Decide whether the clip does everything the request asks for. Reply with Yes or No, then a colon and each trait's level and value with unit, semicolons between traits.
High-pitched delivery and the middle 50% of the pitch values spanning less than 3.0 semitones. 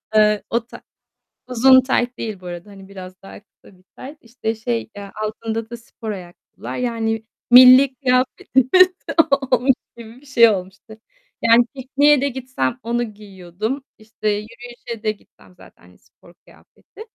No: high, 230 Hz; average, 3.5 semitones